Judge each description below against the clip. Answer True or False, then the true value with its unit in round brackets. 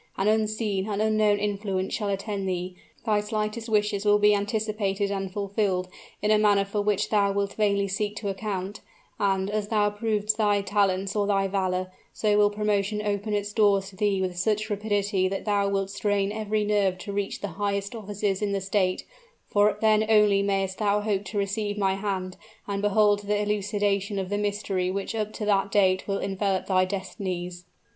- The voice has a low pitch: False (205 Hz)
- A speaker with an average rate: True (185 wpm)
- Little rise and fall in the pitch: True (1.2 semitones)